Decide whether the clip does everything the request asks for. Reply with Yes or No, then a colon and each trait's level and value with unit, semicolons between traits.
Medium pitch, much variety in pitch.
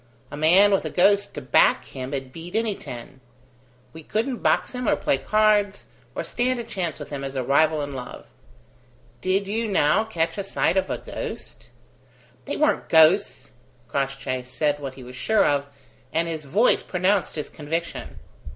Yes: medium, 165 Hz; wide, 6.6 semitones